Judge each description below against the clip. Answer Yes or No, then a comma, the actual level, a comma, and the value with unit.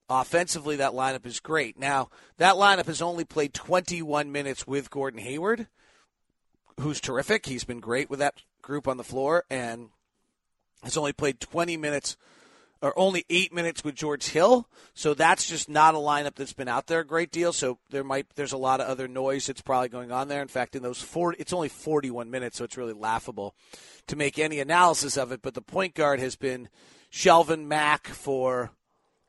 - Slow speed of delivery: No, average, 195 wpm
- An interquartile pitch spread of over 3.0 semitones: Yes, average, 3.7 semitones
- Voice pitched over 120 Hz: Yes, medium, 140 Hz